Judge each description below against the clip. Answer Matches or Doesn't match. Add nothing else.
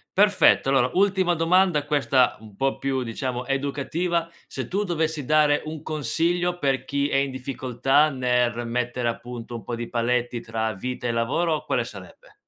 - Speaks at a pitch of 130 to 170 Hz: Matches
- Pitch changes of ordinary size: Matches